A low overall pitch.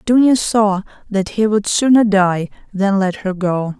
No: high, 205 Hz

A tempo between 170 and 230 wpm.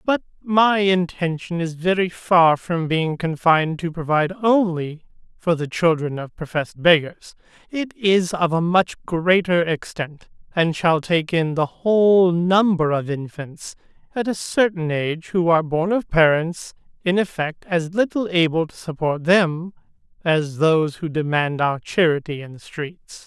No: average, 155 wpm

